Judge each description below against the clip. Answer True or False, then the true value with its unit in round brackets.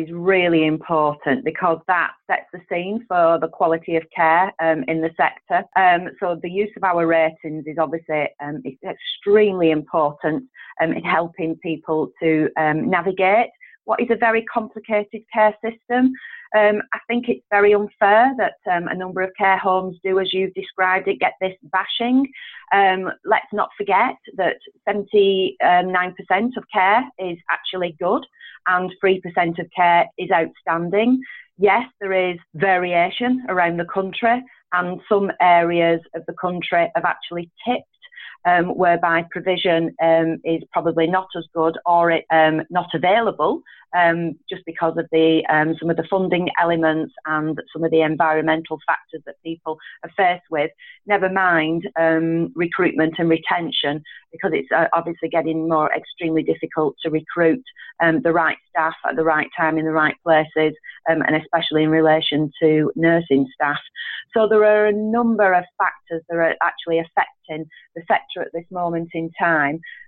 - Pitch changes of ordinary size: True (3.1 semitones)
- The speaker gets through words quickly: False (160 wpm)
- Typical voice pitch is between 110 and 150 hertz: False (175 Hz)